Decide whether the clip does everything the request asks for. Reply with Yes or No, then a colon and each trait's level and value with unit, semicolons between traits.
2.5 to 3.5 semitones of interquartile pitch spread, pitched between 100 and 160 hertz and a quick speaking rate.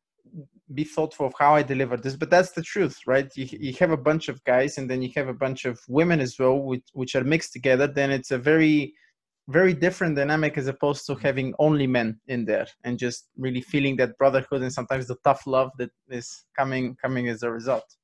Yes: average, 2.8 semitones; low, 135 Hz; fast, 225 wpm